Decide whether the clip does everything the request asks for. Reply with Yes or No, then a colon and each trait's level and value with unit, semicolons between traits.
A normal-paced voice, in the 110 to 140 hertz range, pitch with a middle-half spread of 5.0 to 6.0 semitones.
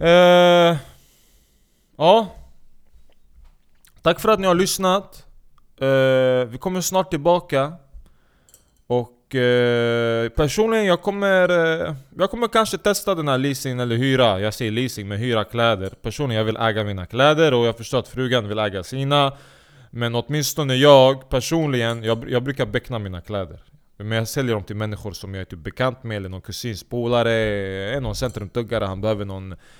Yes: average, 160 wpm; low, 125 Hz; wide, 5.5 semitones